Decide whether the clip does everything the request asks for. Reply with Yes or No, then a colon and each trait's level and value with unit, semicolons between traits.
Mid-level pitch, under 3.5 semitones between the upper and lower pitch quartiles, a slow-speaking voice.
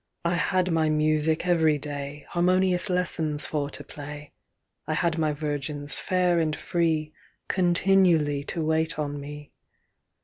Yes: medium, 155 Hz; average, 2.8 semitones; slow, 115 wpm